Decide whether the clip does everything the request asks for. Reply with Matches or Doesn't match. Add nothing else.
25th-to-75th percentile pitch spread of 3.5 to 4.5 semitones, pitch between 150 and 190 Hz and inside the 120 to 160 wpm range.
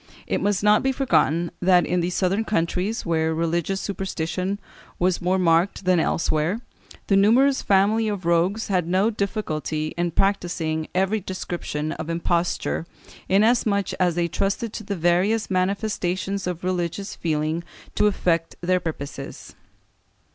Doesn't match